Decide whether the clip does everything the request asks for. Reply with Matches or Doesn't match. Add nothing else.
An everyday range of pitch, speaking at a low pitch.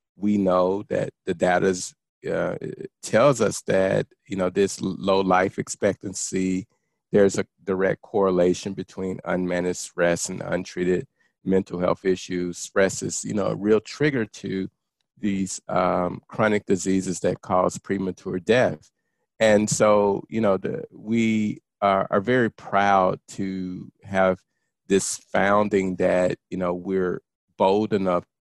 Doesn't match